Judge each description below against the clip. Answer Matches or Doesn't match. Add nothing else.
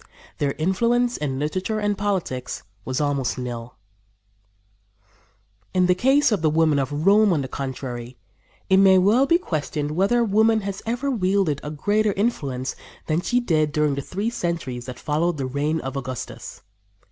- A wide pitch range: Matches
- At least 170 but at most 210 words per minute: Doesn't match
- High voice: Doesn't match